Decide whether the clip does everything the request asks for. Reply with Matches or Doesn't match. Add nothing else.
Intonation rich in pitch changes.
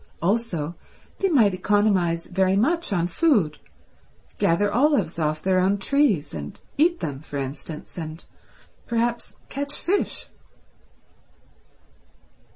Matches